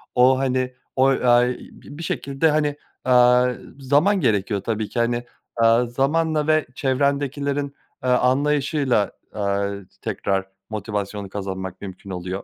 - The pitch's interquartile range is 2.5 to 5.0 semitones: No, wide, 5.4 semitones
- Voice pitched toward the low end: Yes, low, 125 Hz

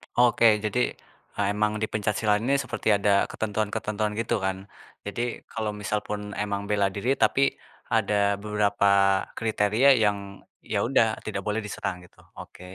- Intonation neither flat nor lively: No, narrow, 1.4 semitones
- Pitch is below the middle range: Yes, low, 105 Hz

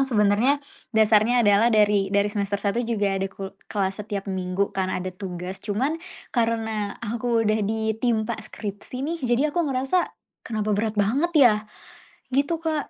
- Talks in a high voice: Yes, high, 215 Hz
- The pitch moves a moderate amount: Yes, average, 3.2 semitones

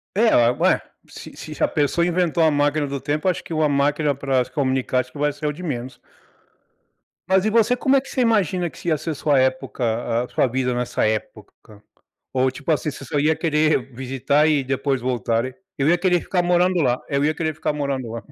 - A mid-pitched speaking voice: Yes, medium, 145 Hz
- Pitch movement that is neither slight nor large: Yes, average, 4.1 semitones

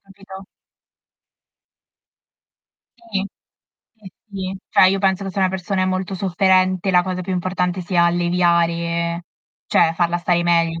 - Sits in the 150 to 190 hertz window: Yes, medium, 185 Hz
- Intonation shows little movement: Yes, narrow, 1.7 semitones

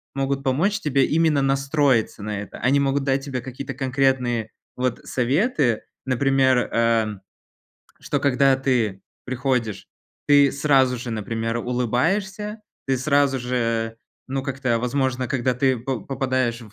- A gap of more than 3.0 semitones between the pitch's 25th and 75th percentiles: No, narrow, 2.4 semitones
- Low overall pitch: Yes, low, 130 Hz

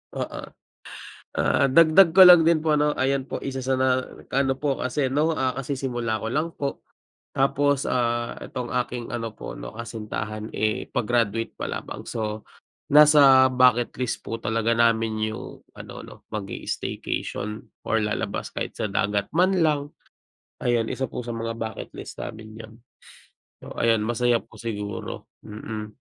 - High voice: No, low, 120 Hz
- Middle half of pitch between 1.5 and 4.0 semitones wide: Yes, average, 3.5 semitones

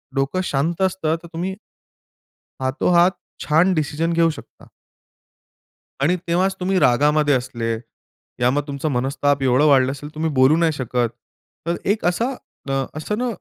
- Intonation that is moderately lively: Yes, average, 4.4 semitones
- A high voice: No, medium, 155 Hz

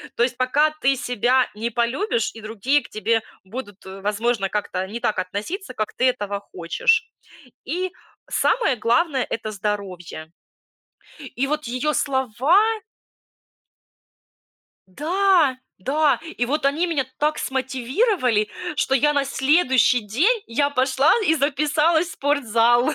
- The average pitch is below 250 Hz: No, very high, 260 Hz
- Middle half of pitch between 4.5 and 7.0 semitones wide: Yes, average, 5.1 semitones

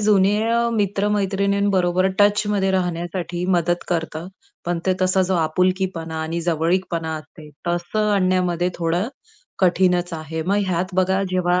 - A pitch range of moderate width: No, narrow, 2.0 semitones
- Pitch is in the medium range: Yes, medium, 180 Hz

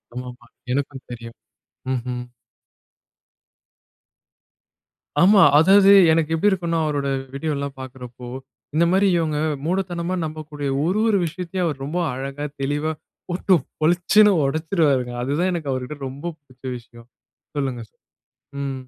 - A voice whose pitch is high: No, medium, 150 Hz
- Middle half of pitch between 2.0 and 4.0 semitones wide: No, average, 4.6 semitones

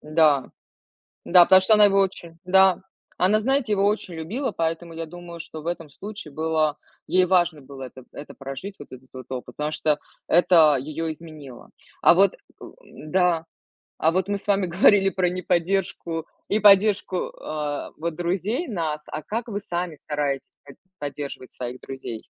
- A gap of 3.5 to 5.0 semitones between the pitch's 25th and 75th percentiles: Yes, average, 4.2 semitones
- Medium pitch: Yes, medium, 170 Hz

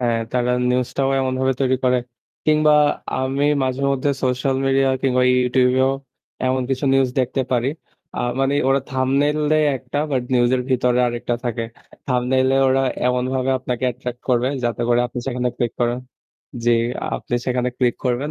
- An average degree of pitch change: No, narrow, 1.4 semitones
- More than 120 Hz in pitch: Yes, low, 130 Hz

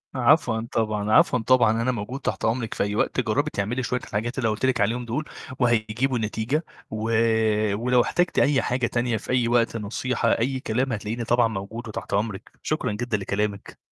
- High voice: No, low, 115 Hz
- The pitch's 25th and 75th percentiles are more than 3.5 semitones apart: No, average, 2.7 semitones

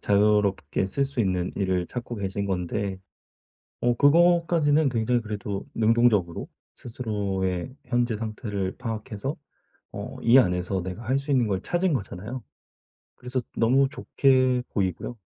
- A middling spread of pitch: Yes, average, 4.9 semitones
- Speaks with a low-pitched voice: Yes, low, 110 Hz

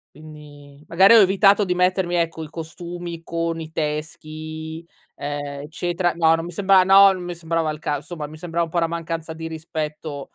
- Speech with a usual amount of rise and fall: No, narrow, 2.2 semitones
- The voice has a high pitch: No, medium, 165 Hz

